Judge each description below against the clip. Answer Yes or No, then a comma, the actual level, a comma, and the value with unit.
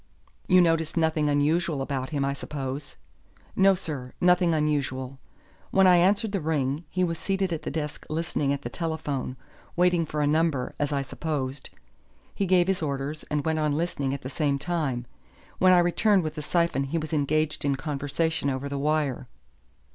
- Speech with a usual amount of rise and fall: Yes, average, 3.3 semitones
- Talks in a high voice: No, medium, 155 Hz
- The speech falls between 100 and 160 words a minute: No, average, 180 wpm